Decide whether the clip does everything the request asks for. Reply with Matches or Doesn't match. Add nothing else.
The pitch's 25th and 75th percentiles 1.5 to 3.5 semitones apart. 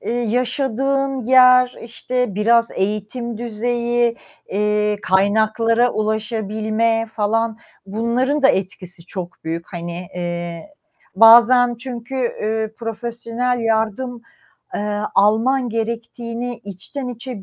Matches